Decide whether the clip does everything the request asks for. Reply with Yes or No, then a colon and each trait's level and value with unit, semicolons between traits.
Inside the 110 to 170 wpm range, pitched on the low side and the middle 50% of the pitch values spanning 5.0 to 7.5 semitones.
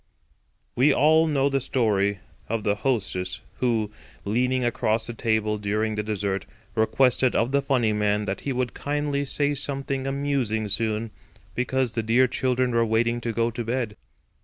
No: average, 160 wpm; low, 115 Hz; average, 3.6 semitones